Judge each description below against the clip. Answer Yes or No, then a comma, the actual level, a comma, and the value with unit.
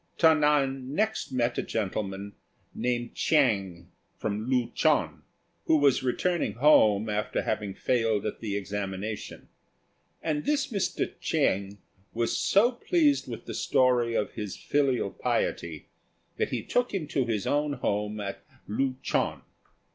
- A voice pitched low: Yes, low, 120 Hz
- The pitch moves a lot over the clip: Yes, wide, 6.1 semitones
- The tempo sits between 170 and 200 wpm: No, average, 140 wpm